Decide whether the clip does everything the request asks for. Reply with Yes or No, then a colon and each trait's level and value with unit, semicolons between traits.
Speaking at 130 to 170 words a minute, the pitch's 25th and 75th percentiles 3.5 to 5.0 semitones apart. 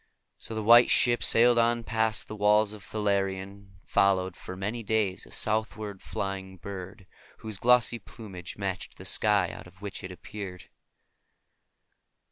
No: average, 155 wpm; narrow, 2.6 semitones